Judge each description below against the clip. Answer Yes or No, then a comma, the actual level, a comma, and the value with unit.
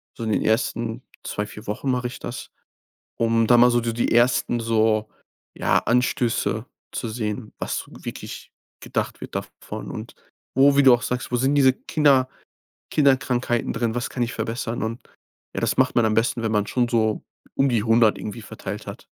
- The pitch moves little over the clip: Yes, narrow, 1.9 semitones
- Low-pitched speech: Yes, low, 120 Hz